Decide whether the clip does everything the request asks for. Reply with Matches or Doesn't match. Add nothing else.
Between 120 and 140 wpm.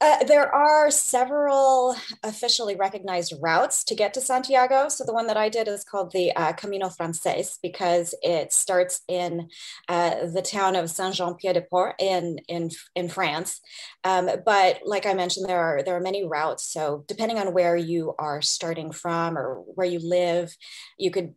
Doesn't match